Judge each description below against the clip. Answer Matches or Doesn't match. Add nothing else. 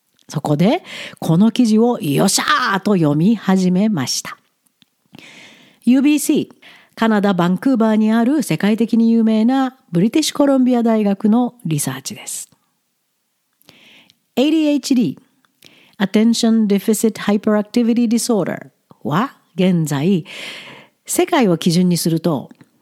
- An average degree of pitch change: Matches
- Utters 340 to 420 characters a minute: Doesn't match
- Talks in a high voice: Matches